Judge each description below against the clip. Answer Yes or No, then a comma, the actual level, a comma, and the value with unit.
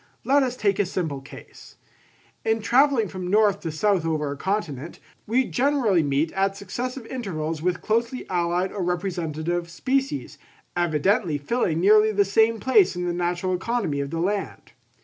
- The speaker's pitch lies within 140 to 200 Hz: Yes, high, 190 Hz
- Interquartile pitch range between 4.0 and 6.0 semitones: Yes, average, 4.7 semitones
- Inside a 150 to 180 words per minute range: Yes, average, 160 wpm